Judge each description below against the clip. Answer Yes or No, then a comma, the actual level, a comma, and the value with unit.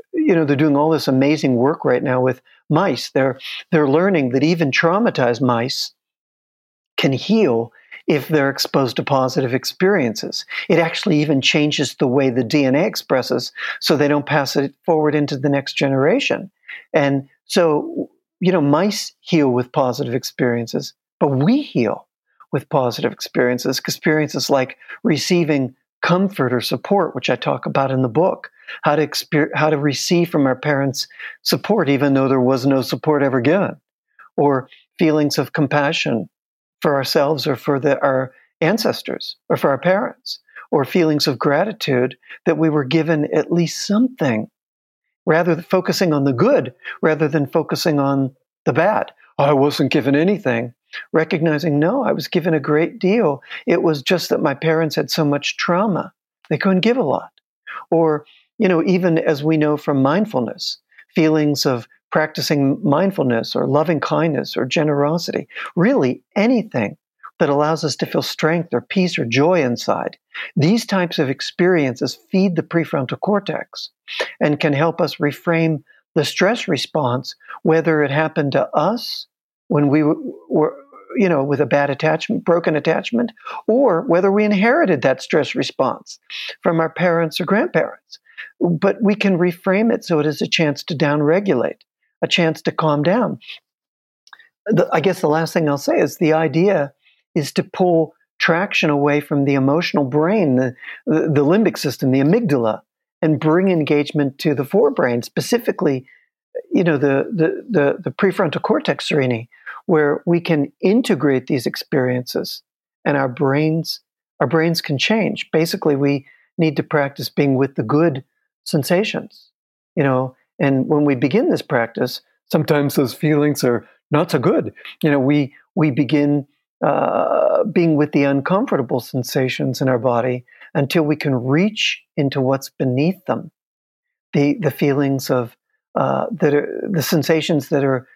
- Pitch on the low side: No, medium, 150 Hz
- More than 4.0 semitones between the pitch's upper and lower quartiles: No, average, 3.5 semitones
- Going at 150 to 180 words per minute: Yes, average, 160 wpm